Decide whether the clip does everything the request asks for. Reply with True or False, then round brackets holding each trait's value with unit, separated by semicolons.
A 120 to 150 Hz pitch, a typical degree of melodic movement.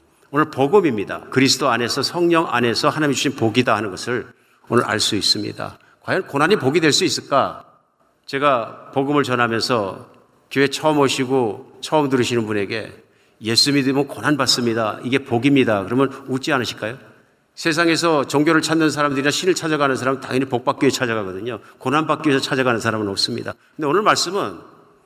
True (135 Hz; 3.3 semitones)